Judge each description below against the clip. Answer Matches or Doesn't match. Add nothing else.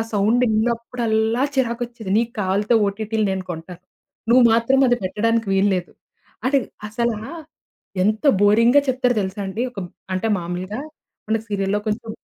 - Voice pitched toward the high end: Matches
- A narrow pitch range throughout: Doesn't match